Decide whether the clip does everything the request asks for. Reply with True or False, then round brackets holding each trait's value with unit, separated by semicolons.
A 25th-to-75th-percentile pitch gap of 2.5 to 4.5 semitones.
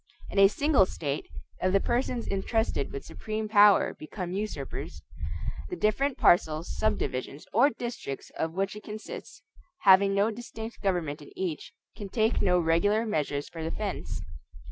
False (5.0 semitones)